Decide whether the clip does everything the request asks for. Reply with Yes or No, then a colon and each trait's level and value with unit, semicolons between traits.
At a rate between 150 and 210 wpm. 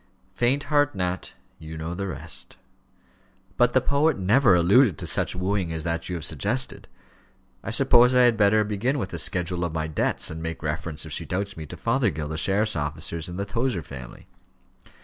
Yes: average, 190 wpm